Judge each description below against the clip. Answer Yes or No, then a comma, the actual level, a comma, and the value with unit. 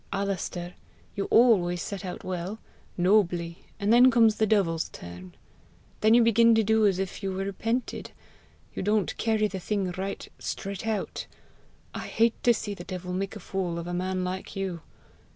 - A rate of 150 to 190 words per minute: Yes, average, 170 wpm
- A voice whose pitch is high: Yes, high, 195 Hz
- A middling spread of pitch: Yes, average, 3.2 semitones